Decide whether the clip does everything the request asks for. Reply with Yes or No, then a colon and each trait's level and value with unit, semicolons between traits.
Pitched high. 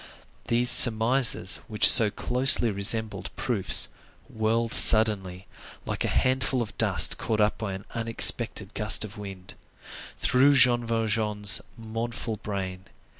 No: low, 110 Hz